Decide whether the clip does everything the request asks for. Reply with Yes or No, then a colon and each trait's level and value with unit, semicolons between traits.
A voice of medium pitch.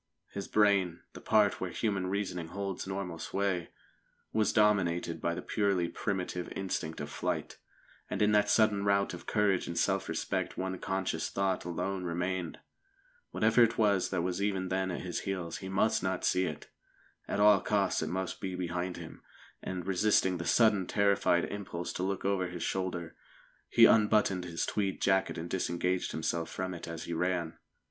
No: very low, 95 Hz